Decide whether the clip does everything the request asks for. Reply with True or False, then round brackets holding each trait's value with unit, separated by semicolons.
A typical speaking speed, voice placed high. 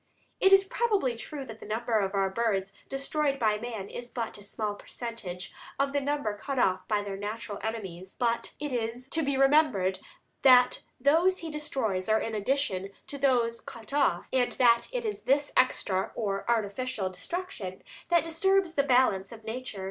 True (180 wpm; 235 Hz)